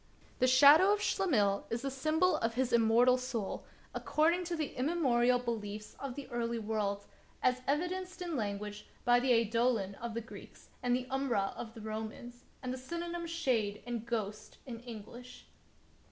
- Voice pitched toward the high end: Yes, high, 245 Hz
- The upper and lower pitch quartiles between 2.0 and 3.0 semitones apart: No, average, 3.8 semitones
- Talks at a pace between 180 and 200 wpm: No, average, 170 wpm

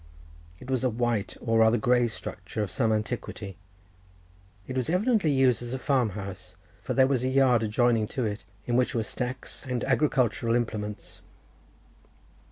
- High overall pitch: No, low, 120 Hz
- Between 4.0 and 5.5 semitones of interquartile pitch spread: No, average, 3.1 semitones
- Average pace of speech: Yes, average, 165 wpm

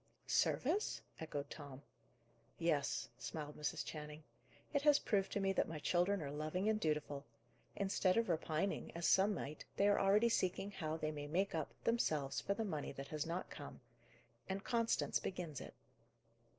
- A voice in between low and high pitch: Yes, medium, 170 Hz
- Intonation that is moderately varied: Yes, average, 4.9 semitones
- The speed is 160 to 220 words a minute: Yes, average, 165 wpm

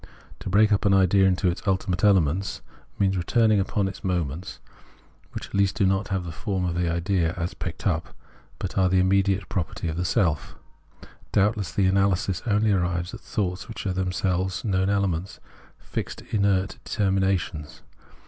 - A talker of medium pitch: No, very low, 95 Hz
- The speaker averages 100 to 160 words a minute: No, average, 170 wpm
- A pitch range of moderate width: No, narrow, 1.8 semitones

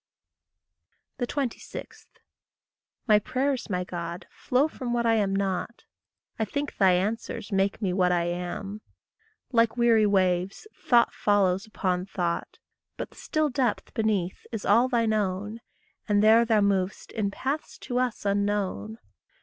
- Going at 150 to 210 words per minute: No, average, 140 wpm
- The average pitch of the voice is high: Yes, high, 210 Hz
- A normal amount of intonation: Yes, average, 3.9 semitones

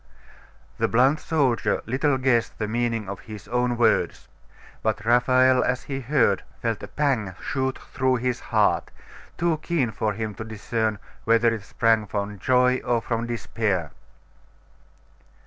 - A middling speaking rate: Yes, average, 145 wpm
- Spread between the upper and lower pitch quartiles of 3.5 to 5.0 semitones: No, average, 2.7 semitones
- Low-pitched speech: Yes, low, 120 Hz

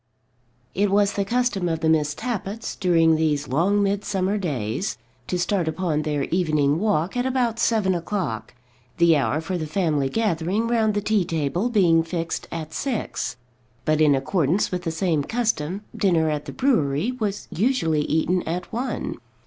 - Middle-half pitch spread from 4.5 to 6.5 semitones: Yes, average, 4.8 semitones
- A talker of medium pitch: Yes, medium, 180 Hz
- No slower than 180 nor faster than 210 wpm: No, average, 165 wpm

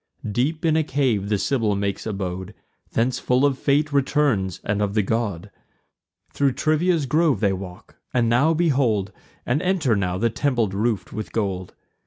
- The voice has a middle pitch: No, low, 115 Hz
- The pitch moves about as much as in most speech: No, wide, 6.1 semitones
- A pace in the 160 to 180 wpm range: Yes, average, 165 wpm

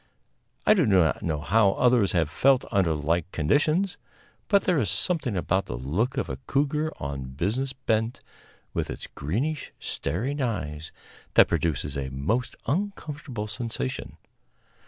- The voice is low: Yes, low, 110 Hz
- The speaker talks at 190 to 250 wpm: No, average, 140 wpm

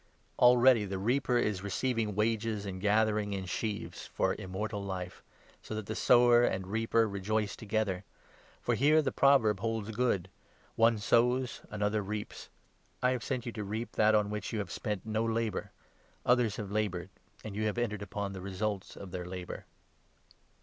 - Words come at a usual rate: Yes, average, 175 wpm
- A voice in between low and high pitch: No, low, 105 Hz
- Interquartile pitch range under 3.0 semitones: Yes, narrow, 2.4 semitones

